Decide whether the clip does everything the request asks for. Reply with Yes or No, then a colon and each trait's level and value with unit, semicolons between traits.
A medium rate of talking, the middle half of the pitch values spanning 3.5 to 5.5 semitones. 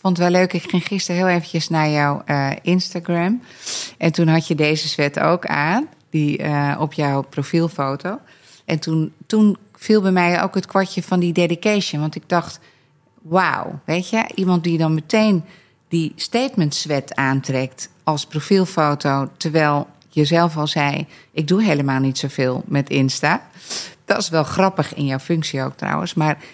Yes: average, 170 wpm; average, 3.9 semitones